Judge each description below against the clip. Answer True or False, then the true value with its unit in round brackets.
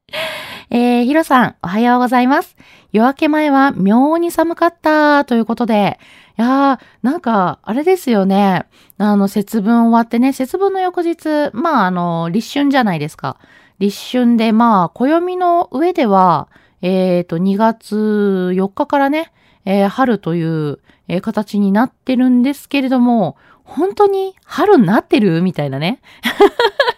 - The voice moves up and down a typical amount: False (6.7 semitones)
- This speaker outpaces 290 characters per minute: False (270 characters per minute)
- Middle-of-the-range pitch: False (240 Hz)